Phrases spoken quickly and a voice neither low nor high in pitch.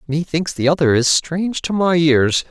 No: average, 190 wpm; medium, 160 Hz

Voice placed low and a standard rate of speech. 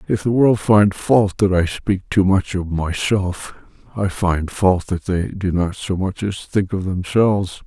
Yes: very low, 95 Hz; average, 195 wpm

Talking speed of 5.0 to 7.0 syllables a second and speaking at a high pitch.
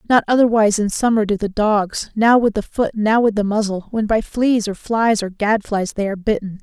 Yes: 5.2 syllables/s; high, 215 Hz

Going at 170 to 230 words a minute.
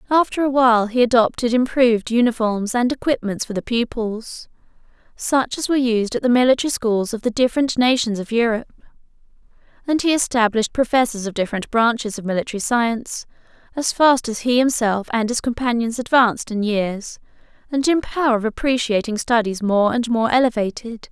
No: average, 160 wpm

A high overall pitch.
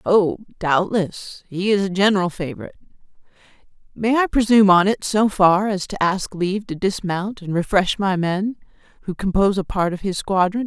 Yes: high, 195 Hz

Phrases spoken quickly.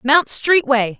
No: average, 180 wpm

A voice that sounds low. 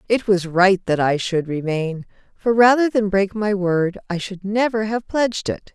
No: high, 200 Hz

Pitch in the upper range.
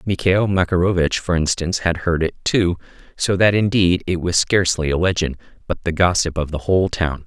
No: very low, 85 Hz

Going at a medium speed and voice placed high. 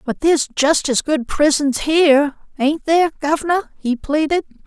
Yes: average, 155 wpm; very high, 300 Hz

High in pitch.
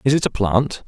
No: low, 120 Hz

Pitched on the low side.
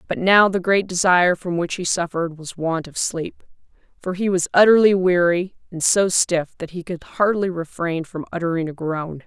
No: medium, 175 Hz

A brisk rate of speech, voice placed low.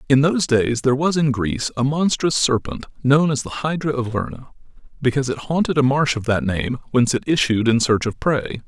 Yes: fast, 215 wpm; low, 130 Hz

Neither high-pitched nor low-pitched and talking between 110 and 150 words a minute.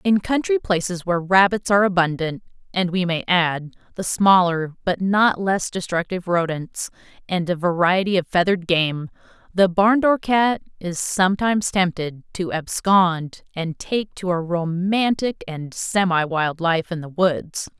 Yes: medium, 180 Hz; average, 145 wpm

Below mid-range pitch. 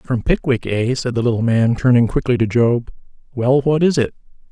Yes: low, 125 Hz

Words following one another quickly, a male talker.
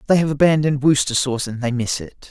Yes: fast, 235 wpm; male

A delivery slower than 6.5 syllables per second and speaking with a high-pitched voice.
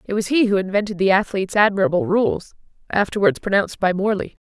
No: 6.7 syllables/s; high, 200 Hz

